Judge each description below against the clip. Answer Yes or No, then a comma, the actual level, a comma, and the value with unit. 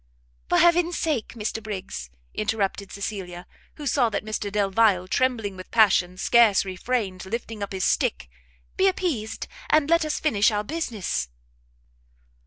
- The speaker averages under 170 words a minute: Yes, average, 140 wpm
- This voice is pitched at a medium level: No, high, 215 Hz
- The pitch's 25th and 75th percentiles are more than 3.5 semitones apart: Yes, average, 4.7 semitones